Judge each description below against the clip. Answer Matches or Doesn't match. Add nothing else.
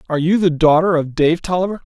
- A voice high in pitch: Doesn't match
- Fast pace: Matches